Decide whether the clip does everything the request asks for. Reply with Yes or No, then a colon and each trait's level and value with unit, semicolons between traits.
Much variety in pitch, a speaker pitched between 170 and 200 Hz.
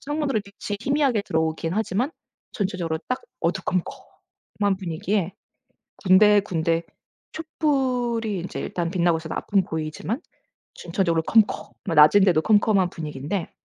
No: average, 4.7 semitones; high, 190 Hz